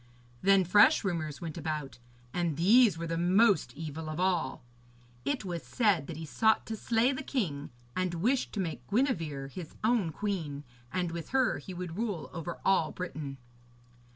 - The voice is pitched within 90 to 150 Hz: No, medium, 175 Hz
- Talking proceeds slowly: No, average, 170 wpm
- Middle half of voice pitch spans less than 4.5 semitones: No, average, 4.9 semitones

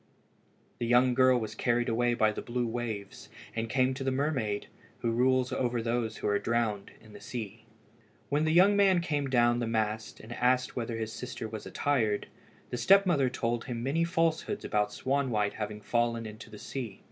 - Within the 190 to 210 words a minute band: Yes, average, 195 wpm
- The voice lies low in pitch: Yes, low, 120 Hz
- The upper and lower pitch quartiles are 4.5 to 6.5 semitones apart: No, average, 2.9 semitones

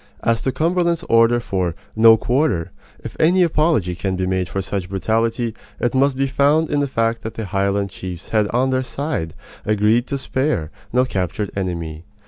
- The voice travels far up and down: Yes, wide, 5.9 semitones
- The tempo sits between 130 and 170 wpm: No, average, 180 wpm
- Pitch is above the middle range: No, low, 115 Hz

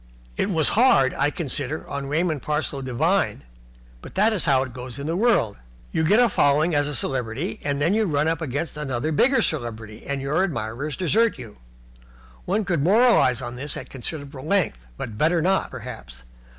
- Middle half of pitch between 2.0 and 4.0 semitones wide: No, average, 4.8 semitones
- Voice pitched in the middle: Yes, medium, 145 Hz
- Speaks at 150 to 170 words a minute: No, average, 185 wpm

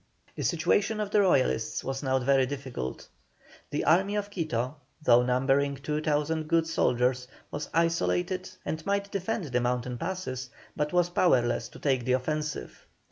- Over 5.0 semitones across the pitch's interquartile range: Yes, wide, 5.5 semitones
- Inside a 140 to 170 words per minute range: Yes, average, 150 wpm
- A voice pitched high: No, medium, 150 Hz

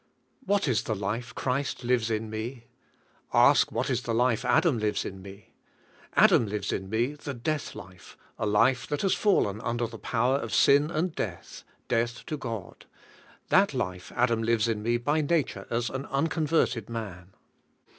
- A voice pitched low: Yes, low, 120 Hz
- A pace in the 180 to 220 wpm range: No, average, 170 wpm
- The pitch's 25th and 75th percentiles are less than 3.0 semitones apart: No, average, 4.1 semitones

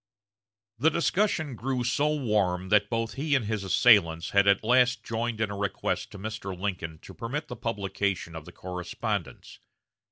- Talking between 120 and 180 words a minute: Yes, average, 160 wpm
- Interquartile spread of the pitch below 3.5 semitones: No, average, 4.2 semitones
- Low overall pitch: Yes, low, 110 Hz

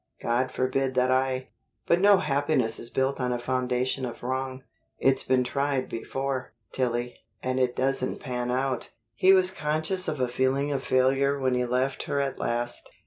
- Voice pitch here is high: No, low, 130 Hz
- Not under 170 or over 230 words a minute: Yes, average, 175 wpm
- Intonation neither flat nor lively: No, narrow, 1.5 semitones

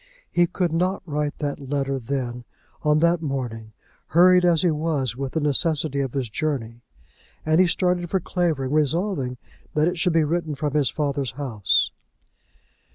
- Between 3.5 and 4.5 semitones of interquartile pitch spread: Yes, average, 3.8 semitones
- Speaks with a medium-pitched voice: Yes, medium, 150 Hz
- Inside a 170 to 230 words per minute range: No, average, 160 wpm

